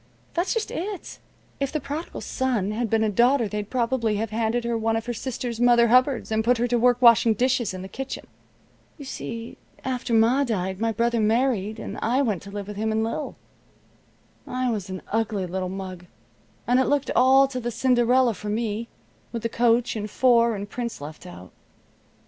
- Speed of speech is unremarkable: Yes, average, 195 wpm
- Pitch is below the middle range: No, high, 230 Hz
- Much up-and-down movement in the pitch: No, average, 2.9 semitones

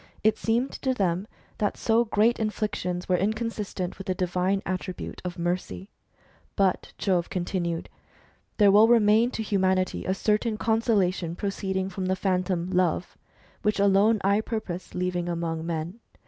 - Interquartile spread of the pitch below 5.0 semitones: Yes, average, 2.9 semitones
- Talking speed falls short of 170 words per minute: Yes, average, 145 wpm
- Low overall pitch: No, high, 190 Hz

